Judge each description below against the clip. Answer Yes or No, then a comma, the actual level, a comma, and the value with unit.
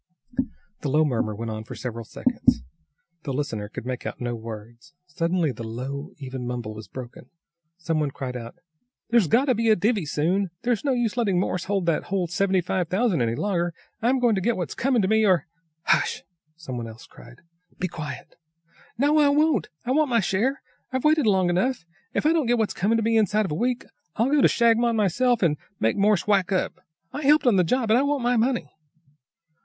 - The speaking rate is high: Yes, fast, 215 wpm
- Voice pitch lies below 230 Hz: Yes, high, 190 Hz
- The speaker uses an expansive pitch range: Yes, wide, 8.8 semitones